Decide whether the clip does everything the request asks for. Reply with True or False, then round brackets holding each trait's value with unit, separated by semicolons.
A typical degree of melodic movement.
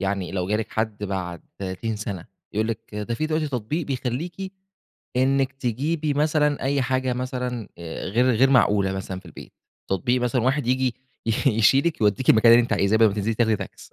True (4.5 semitones)